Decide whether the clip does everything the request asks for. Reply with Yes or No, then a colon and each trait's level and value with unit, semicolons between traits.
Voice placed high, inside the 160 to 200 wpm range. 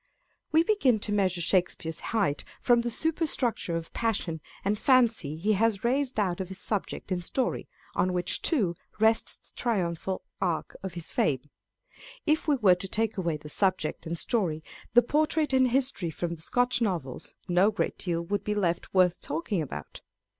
Yes: high, 195 Hz; average, 175 wpm